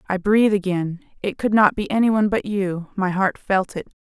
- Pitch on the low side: No, high, 200 Hz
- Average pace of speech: No, fast, 210 wpm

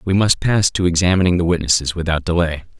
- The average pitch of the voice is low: Yes, very low, 85 Hz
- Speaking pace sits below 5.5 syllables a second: No, 6.2 syllables/s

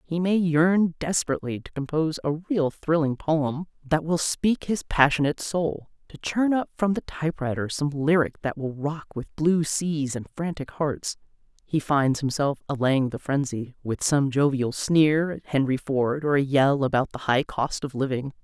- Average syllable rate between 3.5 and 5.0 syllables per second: Yes, 4.6 syllables/s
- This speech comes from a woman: Yes, female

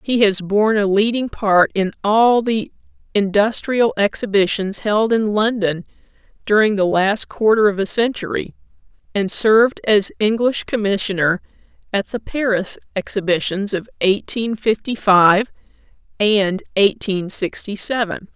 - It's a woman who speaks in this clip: Yes, female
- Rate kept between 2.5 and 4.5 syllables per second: Yes, 4.3 syllables/s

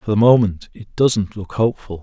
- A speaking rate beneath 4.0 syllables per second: No, 5.3 syllables/s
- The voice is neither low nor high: No, low, 105 Hz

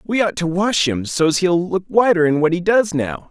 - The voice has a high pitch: No, medium, 175 Hz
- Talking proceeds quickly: Yes, fast, 235 wpm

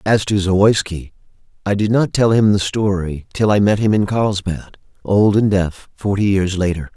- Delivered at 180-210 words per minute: Yes, average, 190 wpm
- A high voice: No, low, 100 Hz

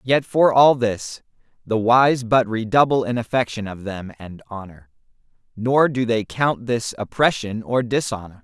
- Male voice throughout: Yes, male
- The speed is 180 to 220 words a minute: No, average, 155 wpm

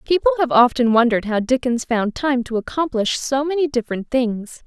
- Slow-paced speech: No, average, 180 wpm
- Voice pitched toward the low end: No, high, 245 Hz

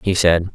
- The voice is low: Yes, very low, 90 Hz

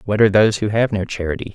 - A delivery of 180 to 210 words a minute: No, fast, 270 wpm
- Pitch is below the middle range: Yes, low, 105 Hz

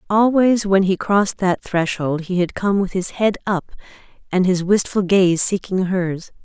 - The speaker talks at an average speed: Yes, average, 175 wpm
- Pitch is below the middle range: No, high, 190 Hz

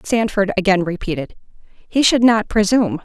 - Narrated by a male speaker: No, female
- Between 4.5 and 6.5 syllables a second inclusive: Yes, 5.2 syllables/s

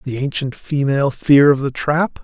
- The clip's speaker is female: No, male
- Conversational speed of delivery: Yes, average, 190 wpm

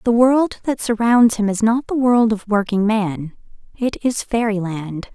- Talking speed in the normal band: Yes, average, 185 wpm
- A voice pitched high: Yes, high, 220 Hz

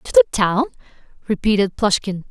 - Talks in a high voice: Yes, high, 215 Hz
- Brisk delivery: No, slow, 130 wpm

